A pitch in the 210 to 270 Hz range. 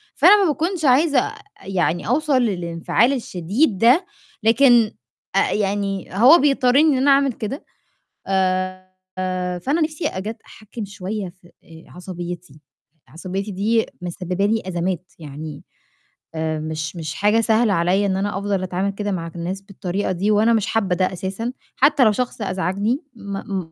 No: high, 200 Hz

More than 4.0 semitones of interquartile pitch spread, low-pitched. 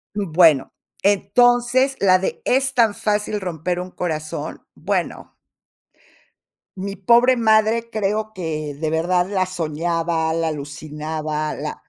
No: average, 5.2 semitones; medium, 185 Hz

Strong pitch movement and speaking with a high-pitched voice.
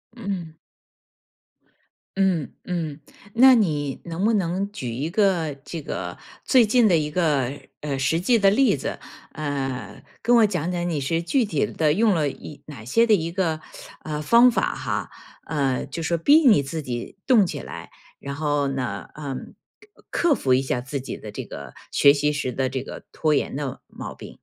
No: wide, 5.8 semitones; medium, 155 Hz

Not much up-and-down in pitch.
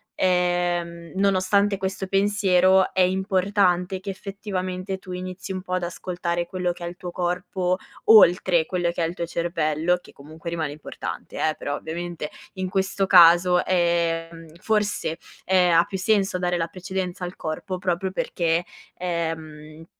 Yes: narrow, 1.8 semitones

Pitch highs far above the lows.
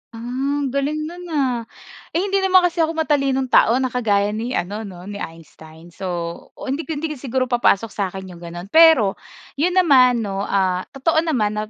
Yes: wide, 7.3 semitones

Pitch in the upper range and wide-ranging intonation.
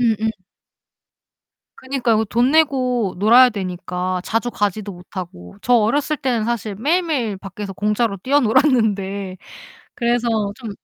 No: high, 220 Hz; average, 3.9 semitones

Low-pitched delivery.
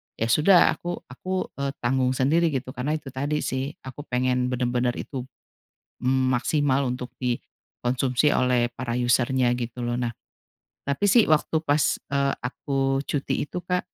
Yes: low, 130 Hz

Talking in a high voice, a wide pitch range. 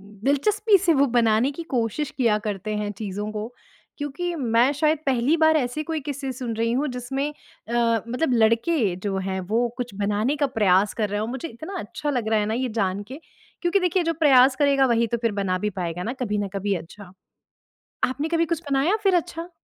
Yes: high, 245 Hz; wide, 5.8 semitones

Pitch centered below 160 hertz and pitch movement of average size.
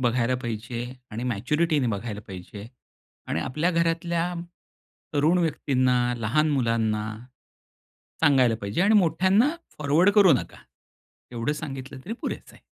No: low, 135 Hz; wide, 6.2 semitones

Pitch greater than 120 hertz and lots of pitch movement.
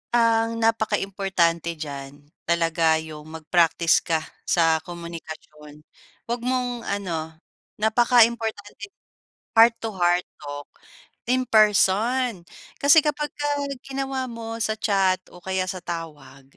Yes: high, 190 Hz; wide, 5.8 semitones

